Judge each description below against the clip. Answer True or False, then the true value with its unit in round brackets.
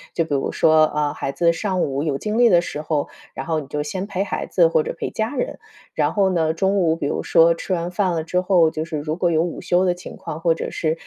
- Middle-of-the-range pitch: True (165 Hz)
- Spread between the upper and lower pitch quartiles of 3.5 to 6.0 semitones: False (2.8 semitones)